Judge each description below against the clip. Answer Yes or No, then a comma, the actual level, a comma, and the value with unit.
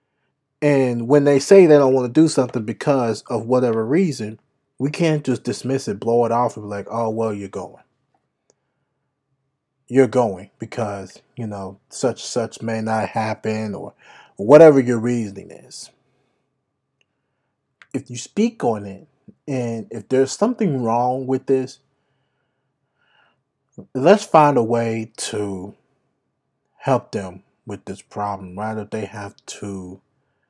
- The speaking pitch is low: Yes, low, 125 Hz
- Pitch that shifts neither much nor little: Yes, average, 4.0 semitones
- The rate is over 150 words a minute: No, average, 140 wpm